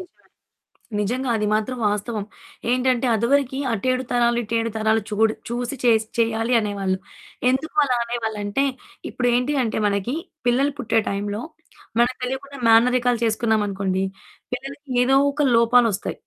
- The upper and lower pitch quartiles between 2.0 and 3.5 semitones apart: Yes, average, 2.8 semitones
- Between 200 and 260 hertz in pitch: Yes, high, 235 Hz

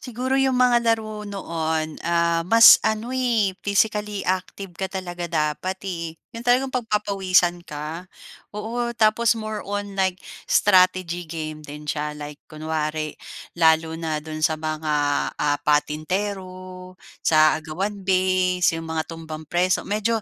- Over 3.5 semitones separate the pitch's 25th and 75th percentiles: Yes, average, 4.8 semitones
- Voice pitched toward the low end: No, medium, 185 Hz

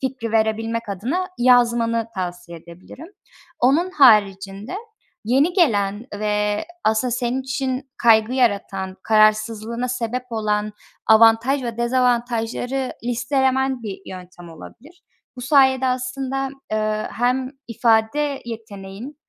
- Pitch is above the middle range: Yes, high, 235 Hz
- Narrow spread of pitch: No, average, 3.4 semitones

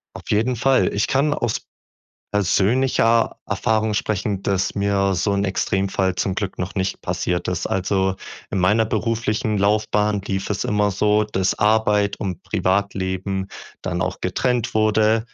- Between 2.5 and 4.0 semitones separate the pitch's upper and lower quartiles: No, narrow, 2.0 semitones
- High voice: No, low, 105 Hz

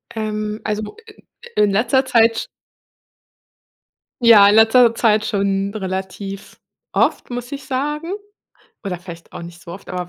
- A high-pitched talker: Yes, high, 215 Hz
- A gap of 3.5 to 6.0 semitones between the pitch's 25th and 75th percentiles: No, average, 3.1 semitones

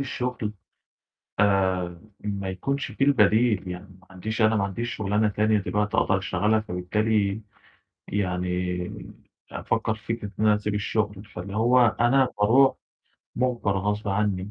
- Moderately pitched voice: No, low, 105 Hz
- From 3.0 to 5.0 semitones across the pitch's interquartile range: No, narrow, 2.4 semitones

